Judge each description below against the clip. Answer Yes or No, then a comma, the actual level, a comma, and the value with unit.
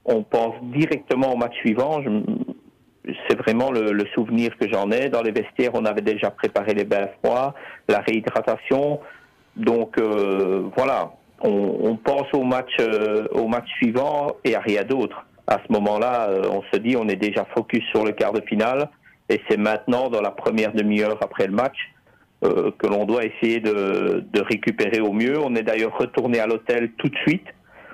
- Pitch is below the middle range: Yes, low, 115 Hz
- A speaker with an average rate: Yes, average, 185 wpm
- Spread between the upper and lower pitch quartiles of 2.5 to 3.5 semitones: Yes, average, 2.8 semitones